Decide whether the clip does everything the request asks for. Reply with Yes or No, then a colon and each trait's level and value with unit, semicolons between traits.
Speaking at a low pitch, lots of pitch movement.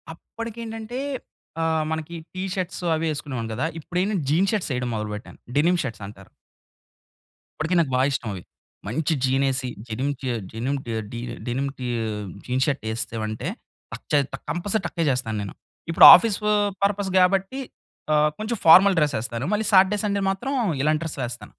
No: medium, 155 Hz; wide, 7.2 semitones